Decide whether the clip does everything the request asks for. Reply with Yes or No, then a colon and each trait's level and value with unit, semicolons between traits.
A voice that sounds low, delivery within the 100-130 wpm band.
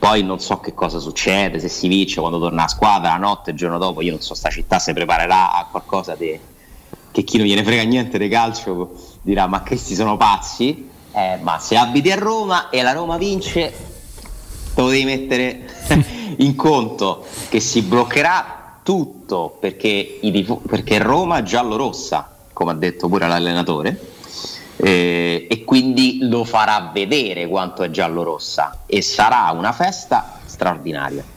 No: low, 100 Hz; fast, 170 wpm